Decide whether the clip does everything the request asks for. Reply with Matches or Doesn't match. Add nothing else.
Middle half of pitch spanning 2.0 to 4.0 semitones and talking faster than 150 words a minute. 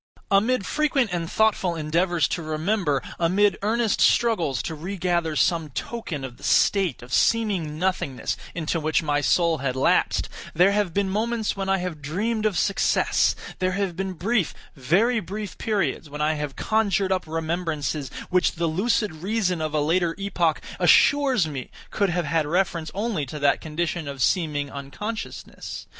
Doesn't match